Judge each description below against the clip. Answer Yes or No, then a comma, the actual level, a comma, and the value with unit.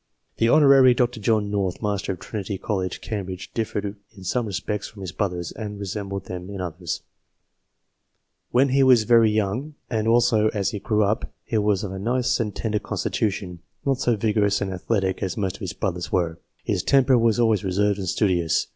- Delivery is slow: No, average, 195 wpm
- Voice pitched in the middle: No, low, 105 Hz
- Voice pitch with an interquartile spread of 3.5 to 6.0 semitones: No, average, 3.1 semitones